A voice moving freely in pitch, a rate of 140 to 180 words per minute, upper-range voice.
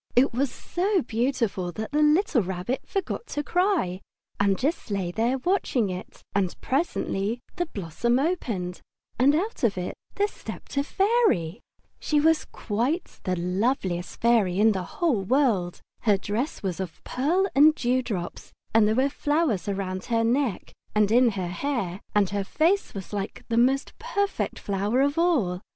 Yes: wide, 7.2 semitones; average, 165 wpm; high, 235 Hz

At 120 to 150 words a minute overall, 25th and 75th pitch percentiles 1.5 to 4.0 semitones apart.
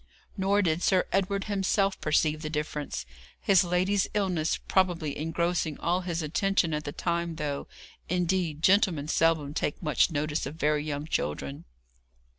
Yes: average, 145 wpm; average, 3.6 semitones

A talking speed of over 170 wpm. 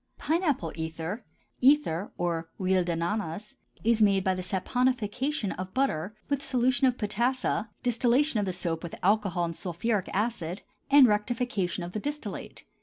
No: average, 150 wpm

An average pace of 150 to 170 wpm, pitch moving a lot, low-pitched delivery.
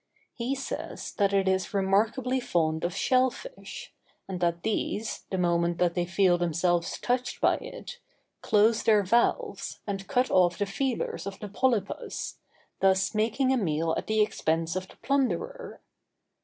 No: average, 155 wpm; wide, 5.8 semitones; high, 200 Hz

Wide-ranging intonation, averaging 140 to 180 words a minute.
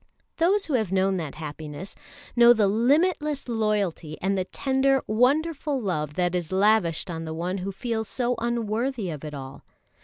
Yes: wide, 6.3 semitones; average, 165 wpm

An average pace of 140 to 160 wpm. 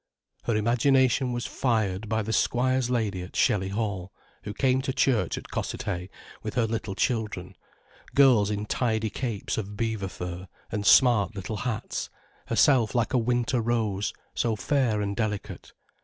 Yes: average, 155 wpm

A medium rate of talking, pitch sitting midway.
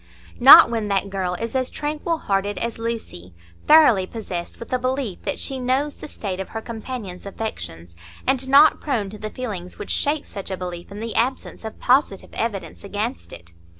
No: average, 185 wpm; high, 220 Hz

